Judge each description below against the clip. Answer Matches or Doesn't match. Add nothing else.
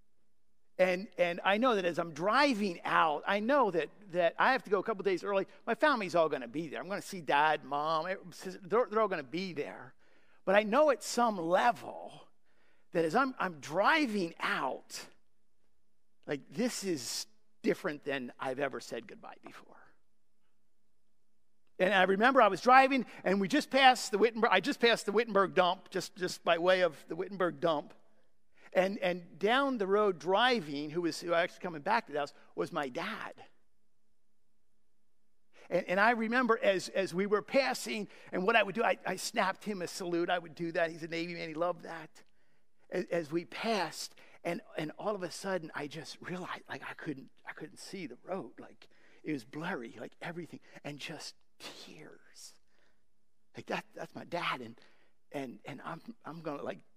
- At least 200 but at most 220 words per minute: Doesn't match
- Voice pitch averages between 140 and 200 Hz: Matches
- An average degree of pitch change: Matches